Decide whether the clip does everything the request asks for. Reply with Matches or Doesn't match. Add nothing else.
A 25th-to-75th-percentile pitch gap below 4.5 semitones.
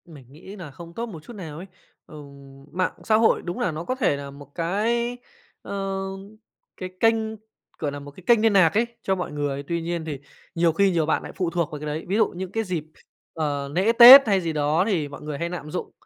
Doesn't match